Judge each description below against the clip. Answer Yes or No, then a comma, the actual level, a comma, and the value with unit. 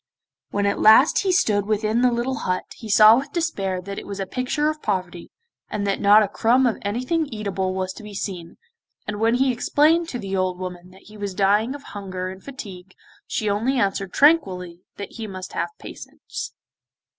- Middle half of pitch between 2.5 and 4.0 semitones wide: No, average, 4.7 semitones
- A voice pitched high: Yes, high, 205 Hz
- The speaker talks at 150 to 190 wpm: No, average, 200 wpm